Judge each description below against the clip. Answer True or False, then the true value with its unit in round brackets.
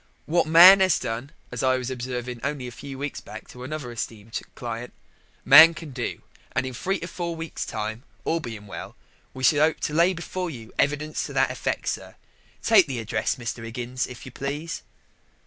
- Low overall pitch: True (130 Hz)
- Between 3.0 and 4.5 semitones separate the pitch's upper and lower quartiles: False (4.9 semitones)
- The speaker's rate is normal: True (195 wpm)